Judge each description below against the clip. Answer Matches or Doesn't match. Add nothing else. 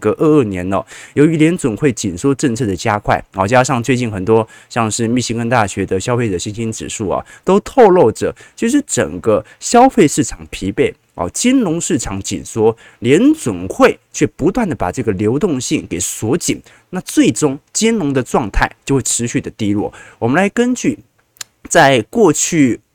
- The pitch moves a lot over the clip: Matches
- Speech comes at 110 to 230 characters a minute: Doesn't match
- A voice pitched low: Matches